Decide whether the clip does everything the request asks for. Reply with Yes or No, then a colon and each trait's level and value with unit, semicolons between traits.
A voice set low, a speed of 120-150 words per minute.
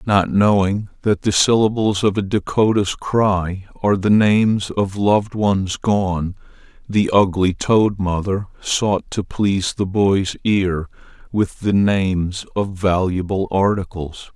Yes: low, 100 Hz; slow, 135 wpm